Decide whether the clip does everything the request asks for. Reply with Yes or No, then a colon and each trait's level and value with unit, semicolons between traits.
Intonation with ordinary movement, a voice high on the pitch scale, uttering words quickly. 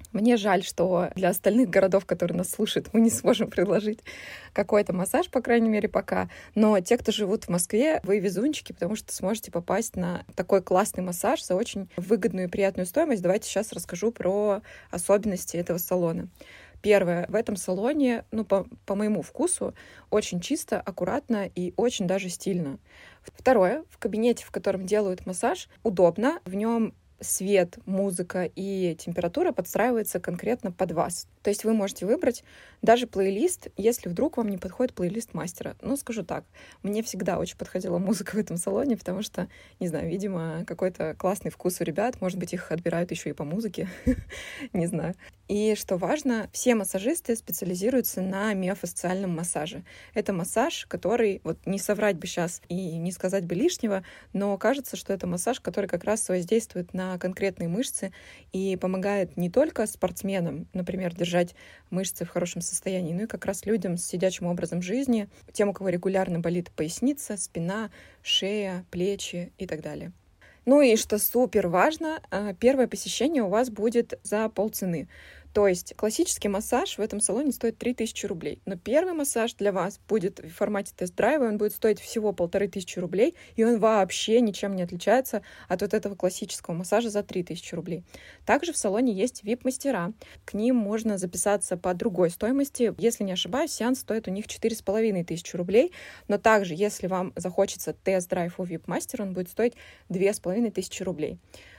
Yes: average, 3.6 semitones; high, 195 Hz; fast, 165 wpm